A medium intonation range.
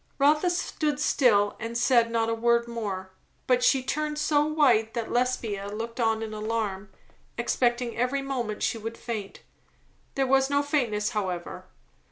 Yes: average, 3.7 semitones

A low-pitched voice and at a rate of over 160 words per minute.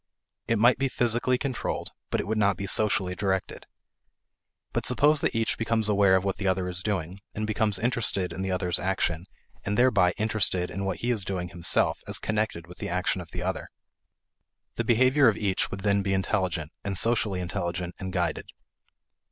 Yes: very low, 95 Hz; average, 190 wpm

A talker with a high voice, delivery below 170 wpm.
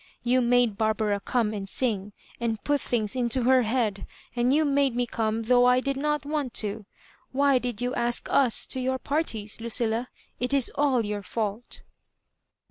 No: high, 245 Hz; average, 175 wpm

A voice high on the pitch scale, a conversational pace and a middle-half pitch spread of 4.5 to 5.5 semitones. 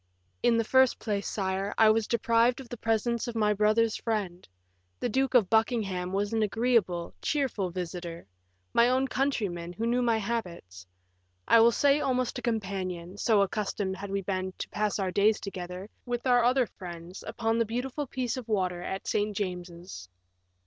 No: high, 215 Hz; average, 175 wpm; average, 4.0 semitones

